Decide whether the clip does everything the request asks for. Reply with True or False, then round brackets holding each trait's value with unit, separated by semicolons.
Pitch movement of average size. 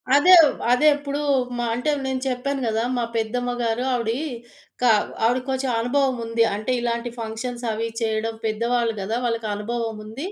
False (2.1 semitones)